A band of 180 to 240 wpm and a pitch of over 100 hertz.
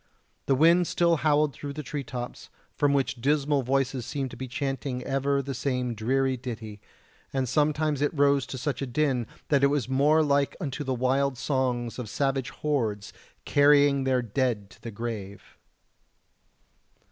No: average, 165 wpm; low, 135 Hz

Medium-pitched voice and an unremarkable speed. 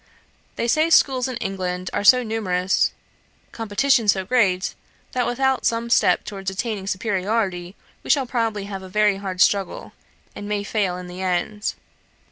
No: high, 205 Hz; average, 160 wpm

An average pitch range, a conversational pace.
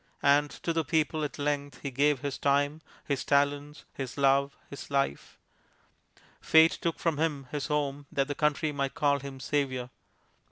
No: narrow, 1.2 semitones; average, 165 wpm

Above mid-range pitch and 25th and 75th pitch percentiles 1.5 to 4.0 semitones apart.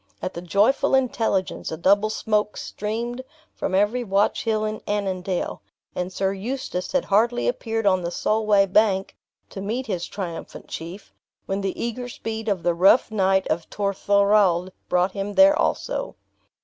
Yes: high, 200 Hz; average, 2.8 semitones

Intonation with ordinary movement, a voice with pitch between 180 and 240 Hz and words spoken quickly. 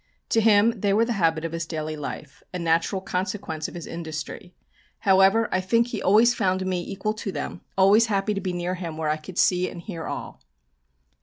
Yes: average, 3.6 semitones; medium, 185 Hz; fast, 210 wpm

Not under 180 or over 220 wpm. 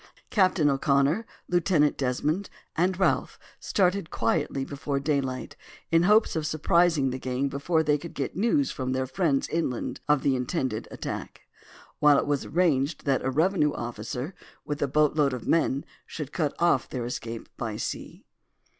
No: average, 160 wpm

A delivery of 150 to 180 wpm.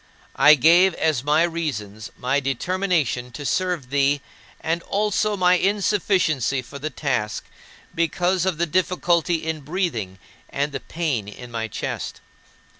No: slow, 135 wpm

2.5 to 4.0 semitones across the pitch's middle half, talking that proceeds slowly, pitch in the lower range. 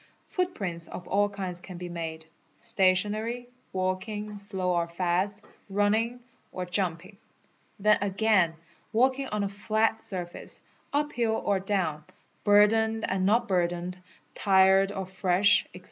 No: average, 3.0 semitones; slow, 130 wpm; high, 195 Hz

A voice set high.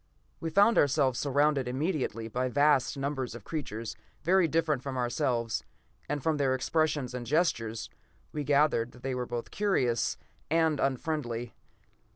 No: low, 135 Hz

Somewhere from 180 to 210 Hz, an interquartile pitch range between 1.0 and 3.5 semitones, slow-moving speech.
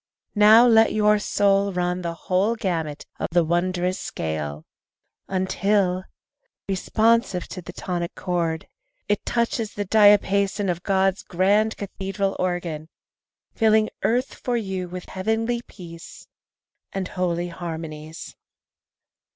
Yes: high, 190 Hz; average, 3.1 semitones; slow, 115 wpm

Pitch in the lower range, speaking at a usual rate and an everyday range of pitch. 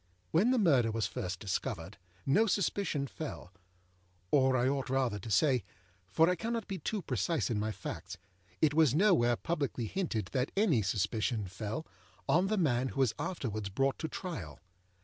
No: low, 130 Hz; average, 160 wpm; wide, 7.4 semitones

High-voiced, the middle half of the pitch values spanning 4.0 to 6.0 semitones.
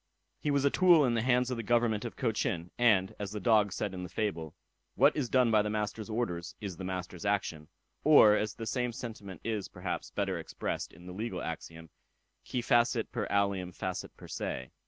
No: low, 105 Hz; average, 4.3 semitones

